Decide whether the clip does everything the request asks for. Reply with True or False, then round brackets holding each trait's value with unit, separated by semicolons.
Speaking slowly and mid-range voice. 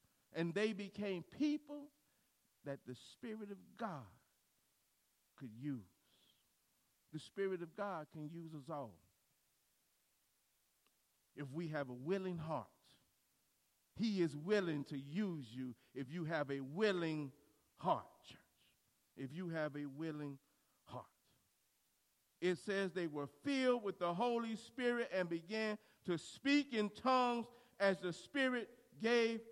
True (130 wpm; 180 Hz)